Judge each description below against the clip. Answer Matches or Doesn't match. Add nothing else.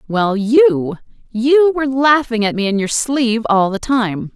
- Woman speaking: Matches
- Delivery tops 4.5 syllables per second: Doesn't match